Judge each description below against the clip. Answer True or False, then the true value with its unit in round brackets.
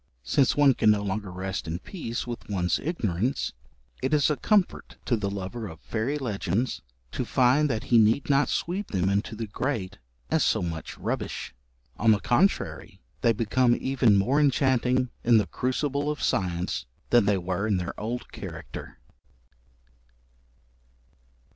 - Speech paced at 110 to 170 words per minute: True (155 wpm)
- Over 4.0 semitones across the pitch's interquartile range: True (5.2 semitones)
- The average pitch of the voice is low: True (115 Hz)